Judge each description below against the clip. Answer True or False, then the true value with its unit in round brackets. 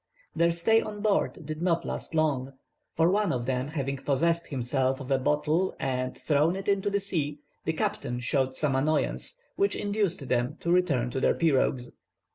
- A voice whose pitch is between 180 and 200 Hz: False (155 Hz)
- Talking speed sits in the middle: True (180 wpm)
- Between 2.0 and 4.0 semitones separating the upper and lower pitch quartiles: False (5.0 semitones)